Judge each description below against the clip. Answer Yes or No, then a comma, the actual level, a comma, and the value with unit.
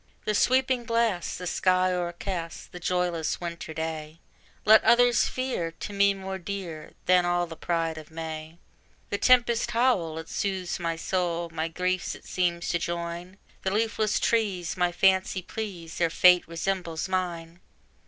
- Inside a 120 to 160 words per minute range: Yes, average, 155 wpm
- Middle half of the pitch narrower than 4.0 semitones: Yes, average, 2.9 semitones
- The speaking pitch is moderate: Yes, medium, 180 Hz